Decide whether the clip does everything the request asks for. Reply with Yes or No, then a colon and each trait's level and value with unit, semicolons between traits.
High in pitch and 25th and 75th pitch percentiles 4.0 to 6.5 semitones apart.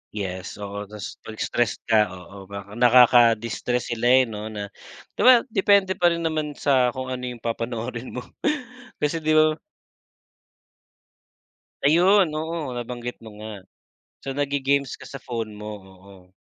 No: low, 125 Hz; average, 4.9 semitones